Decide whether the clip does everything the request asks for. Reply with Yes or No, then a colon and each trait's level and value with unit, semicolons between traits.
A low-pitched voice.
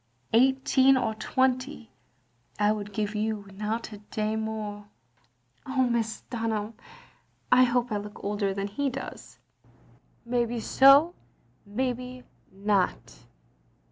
No: high, 220 Hz